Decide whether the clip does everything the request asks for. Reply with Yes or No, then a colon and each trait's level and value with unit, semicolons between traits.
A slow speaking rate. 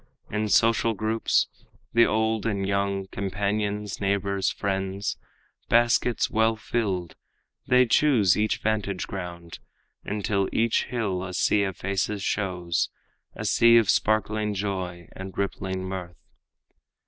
Yes: slow, 120 wpm